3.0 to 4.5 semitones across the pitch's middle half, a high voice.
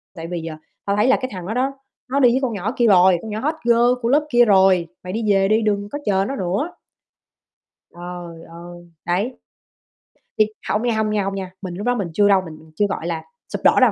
No: average, 4.9 semitones; high, 200 Hz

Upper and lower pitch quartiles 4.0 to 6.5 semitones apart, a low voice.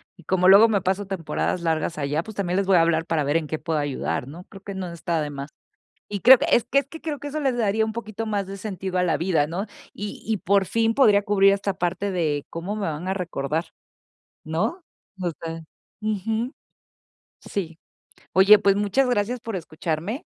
No: average, 4.4 semitones; high, 190 Hz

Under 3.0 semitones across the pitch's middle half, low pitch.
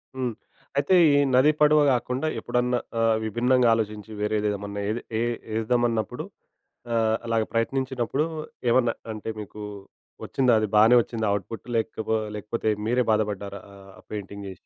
Yes: narrow, 2.6 semitones; low, 115 Hz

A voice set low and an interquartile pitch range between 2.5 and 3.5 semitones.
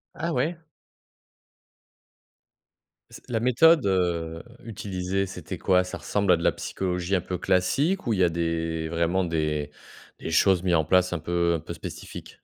Yes: very low, 90 Hz; average, 2.8 semitones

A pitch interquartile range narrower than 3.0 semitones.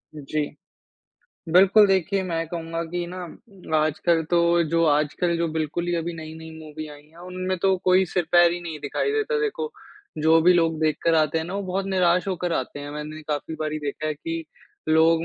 Yes: narrow, 2.6 semitones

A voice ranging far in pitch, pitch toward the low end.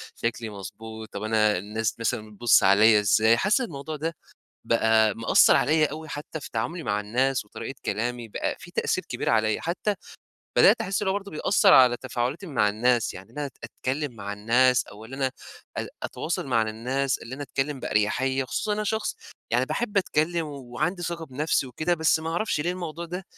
Yes: wide, 6.3 semitones; low, 130 Hz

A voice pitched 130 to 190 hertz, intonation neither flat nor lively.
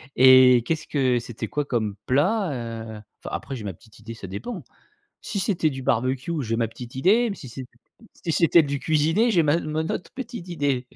No: low, 135 Hz; wide, 6.0 semitones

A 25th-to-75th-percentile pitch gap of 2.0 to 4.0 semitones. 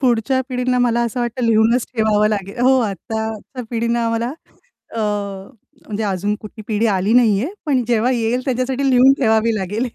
Yes: narrow, 2.5 semitones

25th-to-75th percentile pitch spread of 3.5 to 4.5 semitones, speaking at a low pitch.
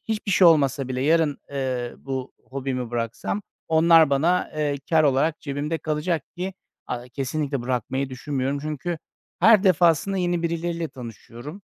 No: average, 4.2 semitones; medium, 150 Hz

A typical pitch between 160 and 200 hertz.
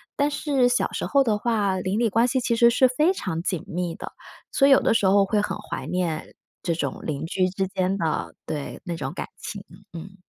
Yes: high, 195 Hz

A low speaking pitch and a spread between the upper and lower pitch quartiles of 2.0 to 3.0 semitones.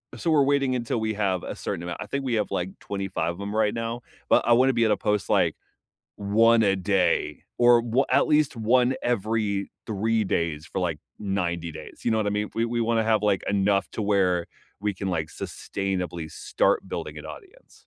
No: low, 105 Hz; average, 3.5 semitones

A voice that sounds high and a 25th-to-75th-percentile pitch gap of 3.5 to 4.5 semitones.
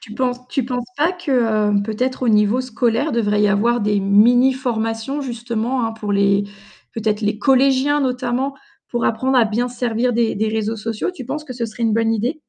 No: high, 235 Hz; average, 2.9 semitones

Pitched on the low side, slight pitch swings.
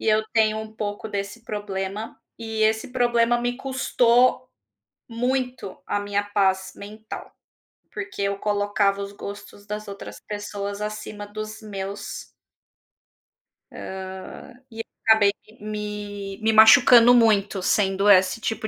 No: high, 210 Hz; narrow, 1.8 semitones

